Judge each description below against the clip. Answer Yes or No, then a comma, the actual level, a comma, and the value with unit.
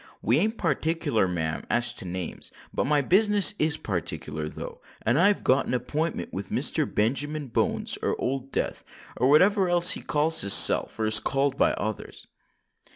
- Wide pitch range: Yes, wide, 7.1 semitones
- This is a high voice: No, low, 135 Hz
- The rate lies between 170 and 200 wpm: No, average, 155 wpm